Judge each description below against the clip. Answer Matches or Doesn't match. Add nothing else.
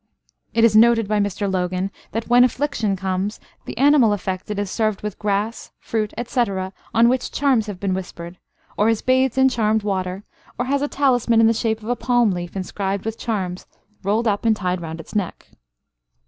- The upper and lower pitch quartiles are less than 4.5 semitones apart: Matches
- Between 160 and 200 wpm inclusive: Matches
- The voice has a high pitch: Matches